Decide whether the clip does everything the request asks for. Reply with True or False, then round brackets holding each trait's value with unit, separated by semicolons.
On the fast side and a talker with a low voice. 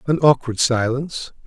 False (125 wpm; 130 Hz)